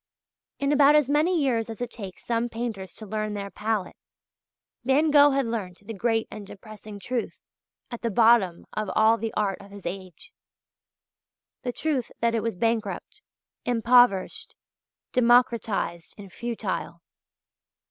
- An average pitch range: Yes, average, 3.1 semitones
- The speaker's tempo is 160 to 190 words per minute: No, average, 145 wpm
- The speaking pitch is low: No, high, 225 Hz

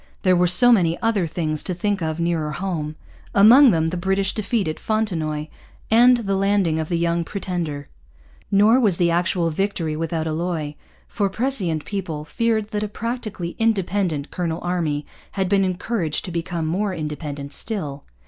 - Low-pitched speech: No, medium, 180 Hz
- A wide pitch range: No, average, 4.2 semitones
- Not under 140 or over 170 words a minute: Yes, average, 165 wpm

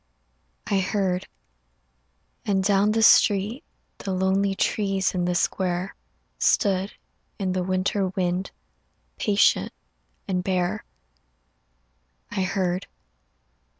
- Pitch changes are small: Yes, narrow, 1.3 semitones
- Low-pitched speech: No, high, 190 Hz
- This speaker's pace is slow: Yes, slow, 95 wpm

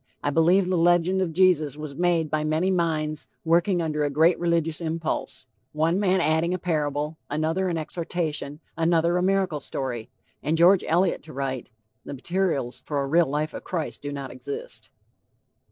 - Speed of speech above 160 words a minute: Yes, average, 170 wpm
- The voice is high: No, medium, 165 Hz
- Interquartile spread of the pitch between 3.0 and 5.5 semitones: No, narrow, 2.6 semitones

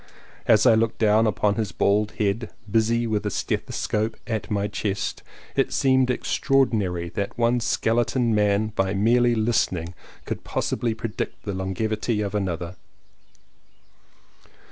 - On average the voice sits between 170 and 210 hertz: No, low, 110 Hz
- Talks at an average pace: No, slow, 130 wpm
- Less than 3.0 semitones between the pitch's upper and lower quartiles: Yes, narrow, 2.4 semitones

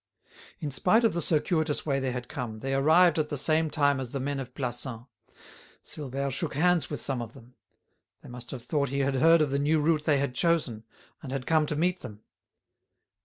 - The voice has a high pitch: No, medium, 140 Hz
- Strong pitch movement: No, average, 3.5 semitones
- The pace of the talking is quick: Yes, fast, 215 wpm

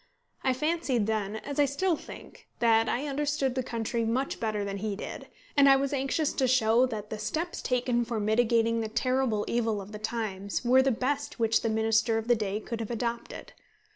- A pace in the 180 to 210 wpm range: Yes, average, 200 wpm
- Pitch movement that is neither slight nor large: Yes, average, 3.2 semitones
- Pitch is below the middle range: No, high, 235 Hz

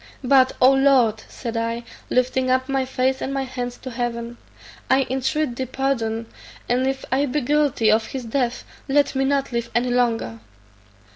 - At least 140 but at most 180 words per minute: Yes, average, 170 wpm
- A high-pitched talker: Yes, very high, 255 Hz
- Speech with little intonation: Yes, narrow, 2.1 semitones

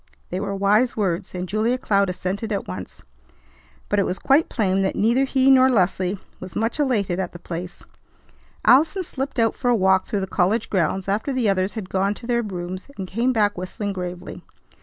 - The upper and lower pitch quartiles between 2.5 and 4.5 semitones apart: Yes, average, 4.1 semitones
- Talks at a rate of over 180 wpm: Yes, average, 200 wpm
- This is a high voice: Yes, high, 200 Hz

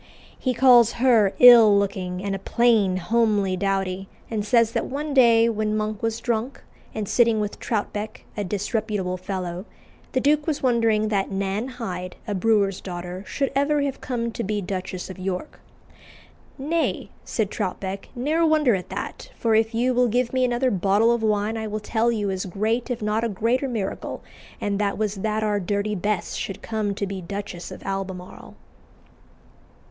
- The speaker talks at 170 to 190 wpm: Yes, average, 175 wpm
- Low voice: No, high, 215 Hz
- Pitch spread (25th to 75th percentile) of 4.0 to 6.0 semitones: No, average, 3.3 semitones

